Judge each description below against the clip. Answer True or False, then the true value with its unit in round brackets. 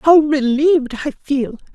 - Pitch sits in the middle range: False (285 Hz)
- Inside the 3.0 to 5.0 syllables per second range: True (4.0 syllables/s)